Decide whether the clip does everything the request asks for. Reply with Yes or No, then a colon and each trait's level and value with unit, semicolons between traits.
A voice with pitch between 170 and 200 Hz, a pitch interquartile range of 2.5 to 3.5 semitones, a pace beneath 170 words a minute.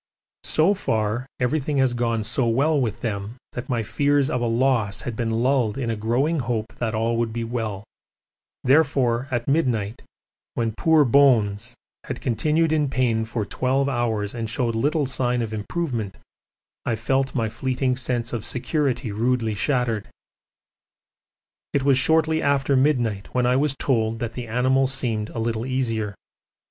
No: low, 120 Hz; average, 3.1 semitones; average, 160 wpm